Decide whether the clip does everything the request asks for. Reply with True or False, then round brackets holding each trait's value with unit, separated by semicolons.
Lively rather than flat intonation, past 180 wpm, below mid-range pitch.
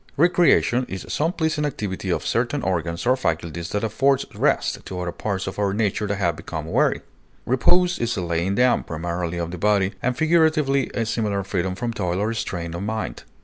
True (6.4 semitones; 190 wpm; 105 Hz)